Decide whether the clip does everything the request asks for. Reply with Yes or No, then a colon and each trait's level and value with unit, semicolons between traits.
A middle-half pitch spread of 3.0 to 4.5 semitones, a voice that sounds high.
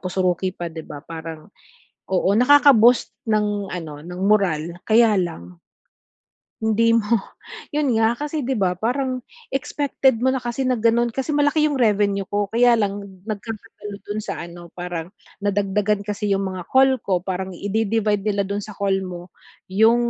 Yes: average, 4.0 semitones; high, 205 Hz